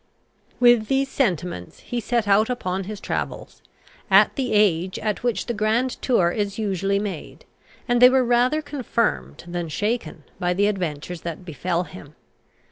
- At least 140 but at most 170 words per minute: Yes, average, 155 wpm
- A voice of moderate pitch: No, high, 205 Hz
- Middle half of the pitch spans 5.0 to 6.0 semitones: Yes, average, 5.3 semitones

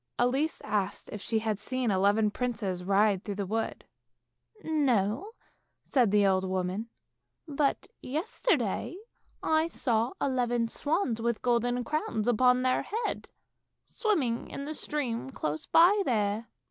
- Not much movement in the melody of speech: No, average, 4.8 semitones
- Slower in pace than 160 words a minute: Yes, slow, 135 wpm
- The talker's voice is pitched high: Yes, high, 235 Hz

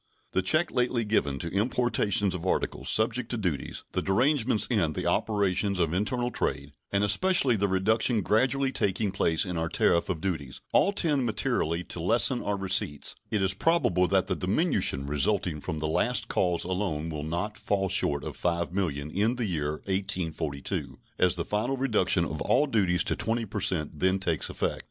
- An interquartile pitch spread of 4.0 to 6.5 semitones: Yes, average, 4.8 semitones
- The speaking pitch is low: Yes, very low, 95 Hz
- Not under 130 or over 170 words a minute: No, average, 180 wpm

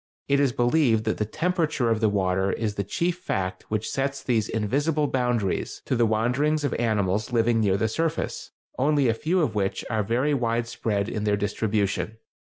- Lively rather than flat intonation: No, average, 4.8 semitones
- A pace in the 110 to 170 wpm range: No, average, 190 wpm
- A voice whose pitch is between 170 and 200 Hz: No, low, 115 Hz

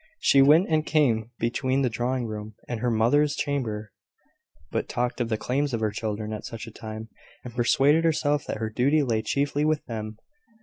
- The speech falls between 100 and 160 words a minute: No, average, 190 wpm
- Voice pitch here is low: Yes, low, 120 Hz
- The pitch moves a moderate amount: Yes, average, 4.5 semitones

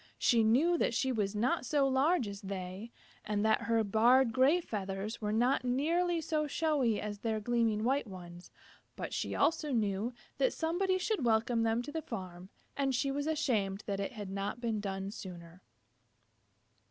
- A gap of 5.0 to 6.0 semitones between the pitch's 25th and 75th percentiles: Yes, wide, 5.4 semitones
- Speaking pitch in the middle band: No, high, 230 Hz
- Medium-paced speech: Yes, average, 175 wpm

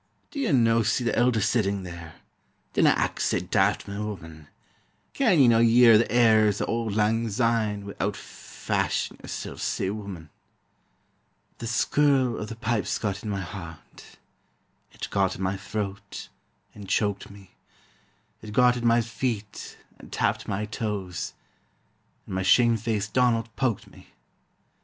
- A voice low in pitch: Yes, low, 105 Hz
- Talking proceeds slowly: No, average, 150 wpm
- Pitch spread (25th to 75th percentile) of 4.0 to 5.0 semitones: No, average, 2.8 semitones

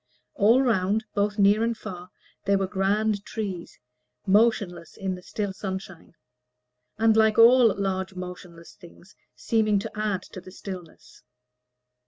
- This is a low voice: No, high, 200 Hz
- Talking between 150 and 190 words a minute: No, slow, 135 wpm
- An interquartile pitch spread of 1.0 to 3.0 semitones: Yes, narrow, 2.6 semitones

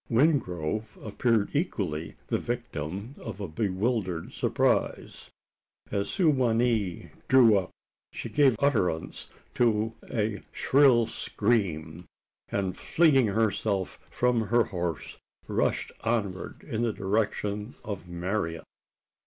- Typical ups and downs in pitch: Yes, average, 4.3 semitones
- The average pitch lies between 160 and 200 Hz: No, low, 105 Hz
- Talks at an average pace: No, slow, 110 wpm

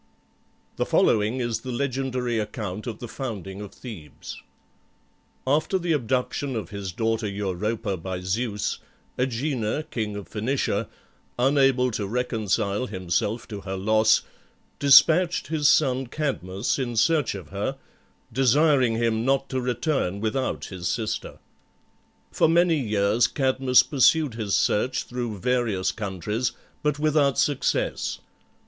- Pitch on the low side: Yes, low, 120 Hz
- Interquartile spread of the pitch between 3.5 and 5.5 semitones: Yes, average, 4.4 semitones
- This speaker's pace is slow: Yes, slow, 125 wpm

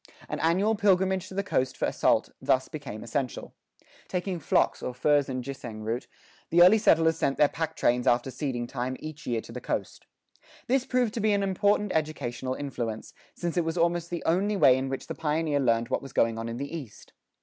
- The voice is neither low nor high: Yes, medium, 150 Hz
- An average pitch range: No, wide, 6.0 semitones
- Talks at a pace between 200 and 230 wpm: Yes, fast, 205 wpm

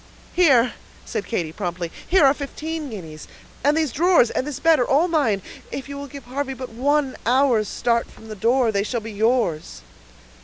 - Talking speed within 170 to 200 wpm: Yes, average, 190 wpm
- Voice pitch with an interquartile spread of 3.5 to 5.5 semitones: Yes, average, 4.7 semitones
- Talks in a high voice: Yes, very high, 255 Hz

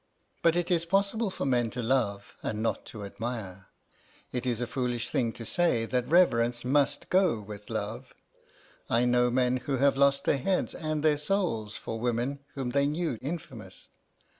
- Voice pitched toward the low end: Yes, low, 125 Hz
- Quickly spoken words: No, average, 175 wpm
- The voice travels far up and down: No, average, 4.6 semitones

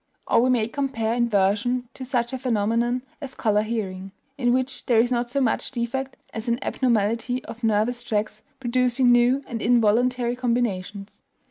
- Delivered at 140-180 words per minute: Yes, average, 160 wpm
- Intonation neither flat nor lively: No, narrow, 2.3 semitones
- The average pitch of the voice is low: No, high, 240 Hz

